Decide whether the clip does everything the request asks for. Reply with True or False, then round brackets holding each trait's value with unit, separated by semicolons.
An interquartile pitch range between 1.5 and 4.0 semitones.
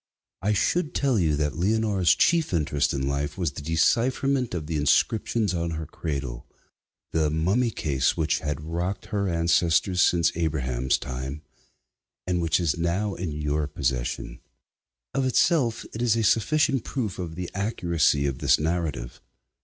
False (5.6 semitones)